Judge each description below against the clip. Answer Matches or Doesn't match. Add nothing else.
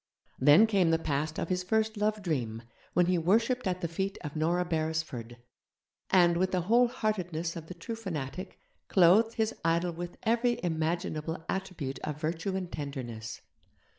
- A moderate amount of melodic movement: Matches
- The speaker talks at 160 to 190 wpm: Matches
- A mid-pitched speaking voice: Matches